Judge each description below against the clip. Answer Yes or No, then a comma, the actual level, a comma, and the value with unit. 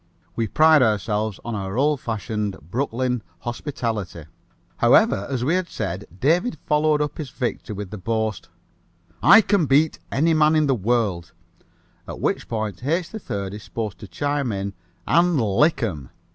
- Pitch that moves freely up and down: Yes, wide, 6.4 semitones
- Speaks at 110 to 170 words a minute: Yes, average, 160 wpm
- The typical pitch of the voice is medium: No, low, 120 Hz